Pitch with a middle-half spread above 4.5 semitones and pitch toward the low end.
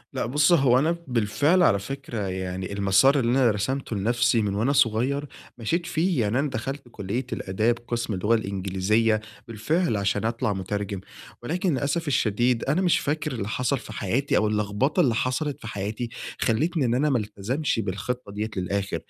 Yes: average, 5.2 semitones; low, 115 Hz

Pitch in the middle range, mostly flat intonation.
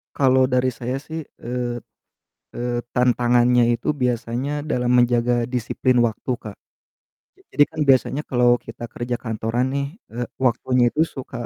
No: low, 125 Hz; narrow, 1.2 semitones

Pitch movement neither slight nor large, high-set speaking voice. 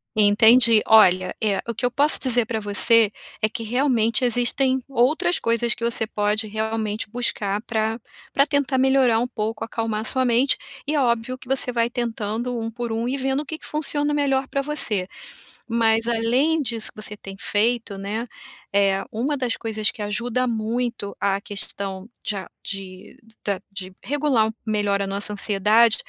Yes: average, 3.0 semitones; high, 230 Hz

